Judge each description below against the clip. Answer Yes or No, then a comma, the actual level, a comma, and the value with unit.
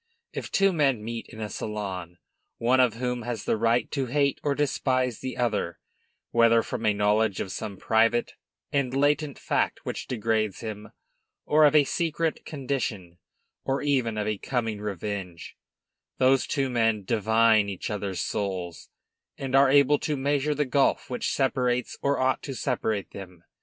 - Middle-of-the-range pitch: No, low, 115 Hz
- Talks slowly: No, average, 165 wpm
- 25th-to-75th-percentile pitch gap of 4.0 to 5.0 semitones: Yes, average, 4.4 semitones